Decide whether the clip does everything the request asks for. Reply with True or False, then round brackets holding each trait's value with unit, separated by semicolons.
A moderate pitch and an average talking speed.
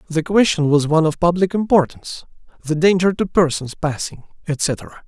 True (165 Hz; 155 wpm)